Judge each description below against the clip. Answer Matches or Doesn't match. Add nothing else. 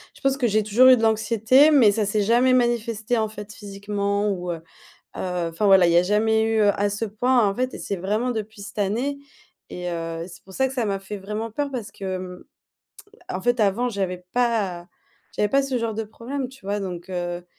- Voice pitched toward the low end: Doesn't match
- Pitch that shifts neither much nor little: Matches